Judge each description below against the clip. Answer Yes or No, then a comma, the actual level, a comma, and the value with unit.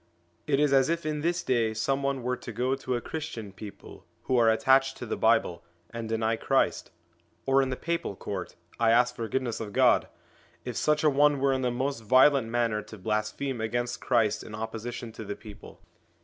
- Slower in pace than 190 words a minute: No, fast, 205 wpm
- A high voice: No, low, 120 Hz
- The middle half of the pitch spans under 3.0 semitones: No, average, 3.4 semitones